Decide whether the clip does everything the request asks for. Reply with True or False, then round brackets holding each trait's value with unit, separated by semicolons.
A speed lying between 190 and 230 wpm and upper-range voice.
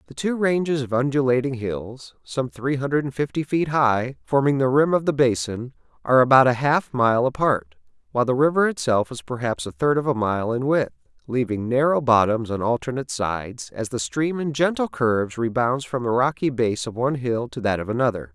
False (205 wpm; 130 Hz)